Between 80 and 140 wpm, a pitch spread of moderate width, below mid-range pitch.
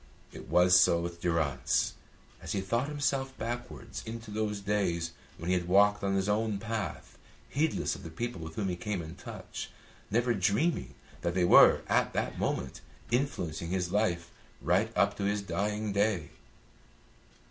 No: average, 165 wpm; average, 4.2 semitones; low, 100 Hz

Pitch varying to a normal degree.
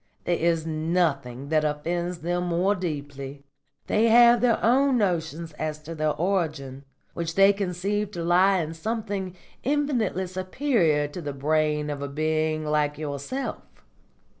Yes: average, 4.4 semitones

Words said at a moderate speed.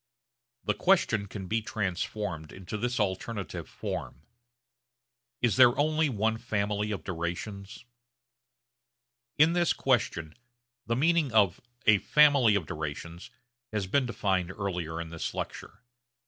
No: slow, 120 wpm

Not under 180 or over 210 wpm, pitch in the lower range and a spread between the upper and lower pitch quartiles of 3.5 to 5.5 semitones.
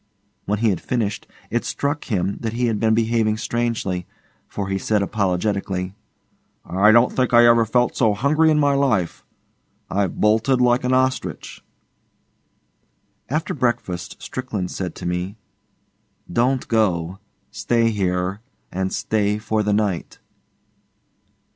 No: slow, 135 wpm; low, 110 Hz; average, 3.8 semitones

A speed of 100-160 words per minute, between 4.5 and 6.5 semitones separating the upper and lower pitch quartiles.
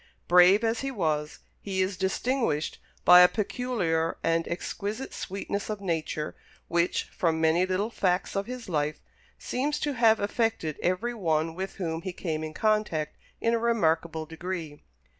Yes: average, 155 wpm; average, 5.2 semitones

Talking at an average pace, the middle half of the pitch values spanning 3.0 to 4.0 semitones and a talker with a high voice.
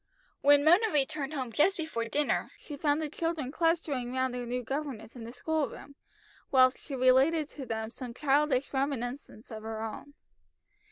Yes: average, 170 wpm; average, 3.5 semitones; very high, 270 Hz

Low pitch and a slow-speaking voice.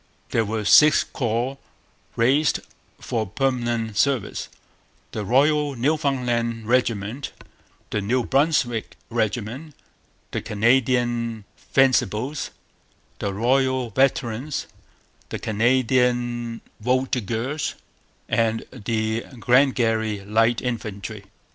Yes: low, 120 Hz; slow, 85 wpm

